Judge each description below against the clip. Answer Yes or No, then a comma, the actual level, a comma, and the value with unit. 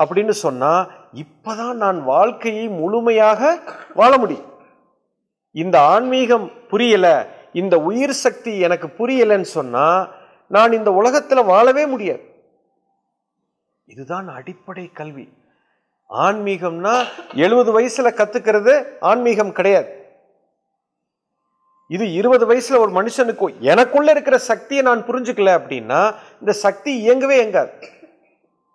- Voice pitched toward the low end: No, high, 230 Hz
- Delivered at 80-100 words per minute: Yes, average, 95 wpm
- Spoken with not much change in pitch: No, average, 4.4 semitones